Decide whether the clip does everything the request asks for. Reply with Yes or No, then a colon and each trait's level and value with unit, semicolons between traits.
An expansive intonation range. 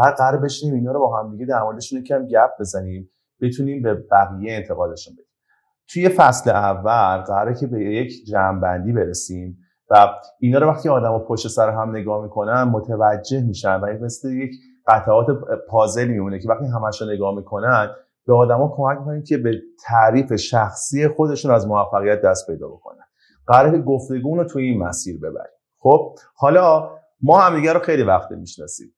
No: average, 4.7 semitones